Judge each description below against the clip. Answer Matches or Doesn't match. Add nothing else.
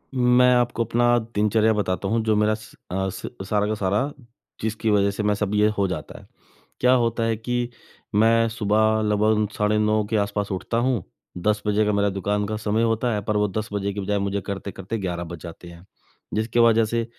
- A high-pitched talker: Doesn't match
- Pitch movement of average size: Doesn't match